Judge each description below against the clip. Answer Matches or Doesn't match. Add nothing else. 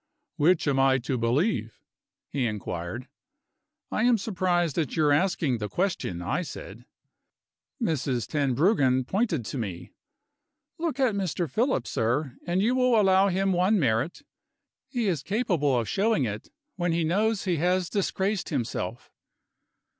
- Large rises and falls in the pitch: Matches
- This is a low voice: Doesn't match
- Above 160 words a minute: Doesn't match